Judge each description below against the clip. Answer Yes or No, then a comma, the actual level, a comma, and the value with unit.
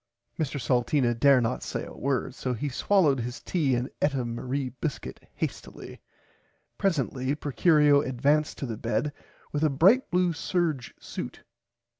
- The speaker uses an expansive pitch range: No, average, 3.3 semitones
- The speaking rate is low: No, average, 150 wpm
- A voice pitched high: No, medium, 140 Hz